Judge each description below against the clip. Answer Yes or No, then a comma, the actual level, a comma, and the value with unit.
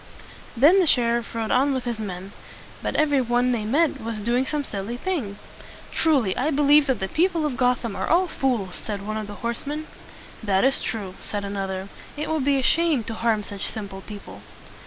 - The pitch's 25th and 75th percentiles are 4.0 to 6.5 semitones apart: Yes, wide, 5.6 semitones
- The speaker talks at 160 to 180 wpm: No, average, 200 wpm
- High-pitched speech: Yes, high, 240 Hz